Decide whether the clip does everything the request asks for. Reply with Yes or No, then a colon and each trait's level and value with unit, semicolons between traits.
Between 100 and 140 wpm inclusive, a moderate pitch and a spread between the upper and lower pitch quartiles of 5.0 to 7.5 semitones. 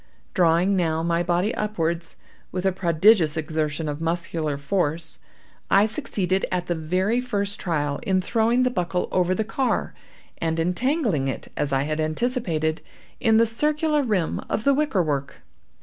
No: average, 155 wpm; medium, 180 Hz; average, 5.3 semitones